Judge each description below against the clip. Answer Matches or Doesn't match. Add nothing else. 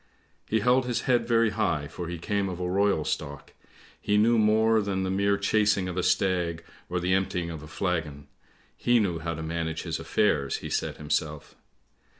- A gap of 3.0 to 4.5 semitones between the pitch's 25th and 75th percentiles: Matches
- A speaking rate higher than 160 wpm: Matches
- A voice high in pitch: Doesn't match